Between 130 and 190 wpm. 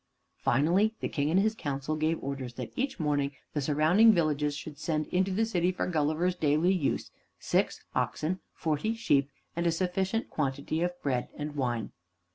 Yes: average, 170 wpm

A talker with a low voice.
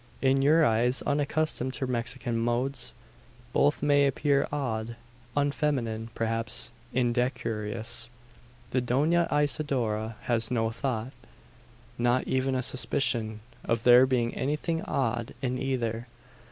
Yes: low, 125 Hz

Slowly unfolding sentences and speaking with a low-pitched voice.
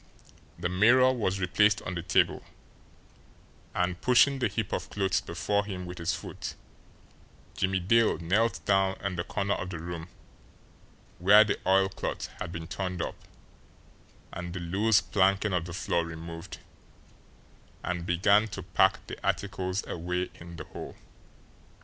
No: average, 145 wpm; very low, 95 Hz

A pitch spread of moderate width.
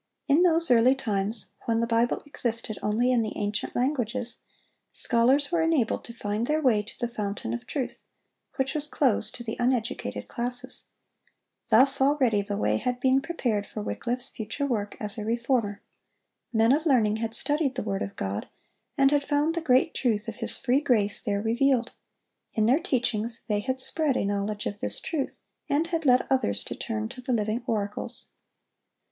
Yes: average, 4.0 semitones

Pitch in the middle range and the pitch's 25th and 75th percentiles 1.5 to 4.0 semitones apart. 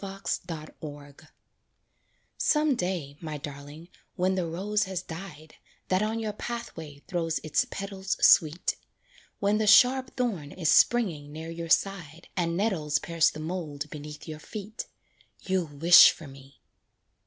No: medium, 170 Hz; average, 4.5 semitones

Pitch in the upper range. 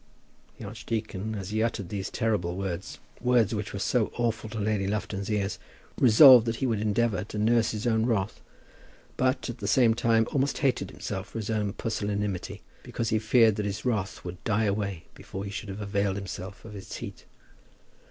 No: low, 105 Hz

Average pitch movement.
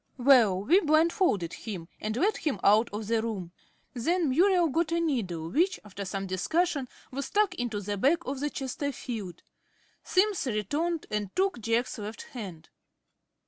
No: wide, 8.2 semitones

